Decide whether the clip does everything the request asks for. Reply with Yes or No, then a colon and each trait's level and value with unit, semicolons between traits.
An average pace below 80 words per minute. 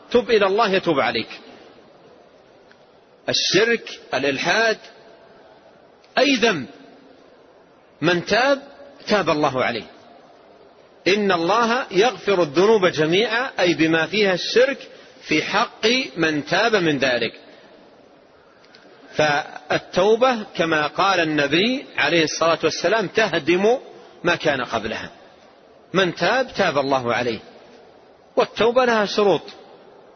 No: average, 95 wpm